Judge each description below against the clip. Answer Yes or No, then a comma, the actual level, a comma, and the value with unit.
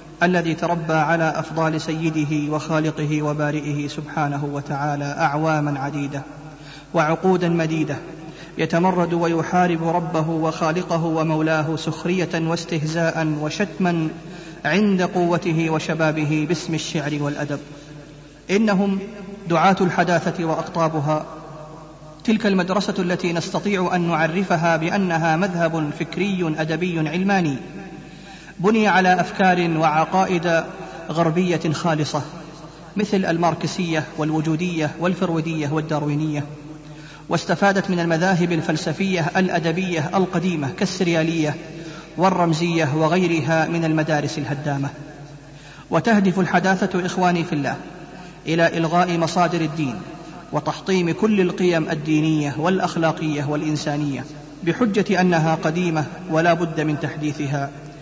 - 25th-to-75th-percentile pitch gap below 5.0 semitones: Yes, narrow, 2.4 semitones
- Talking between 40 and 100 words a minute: Yes, average, 90 wpm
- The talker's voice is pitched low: No, medium, 165 Hz